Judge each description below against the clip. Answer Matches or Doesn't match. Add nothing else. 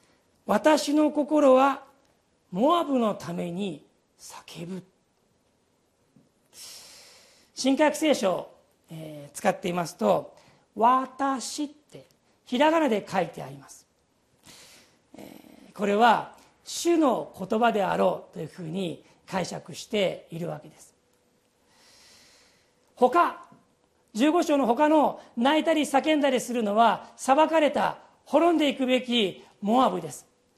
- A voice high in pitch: Matches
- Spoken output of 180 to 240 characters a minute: Matches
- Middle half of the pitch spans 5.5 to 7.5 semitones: Matches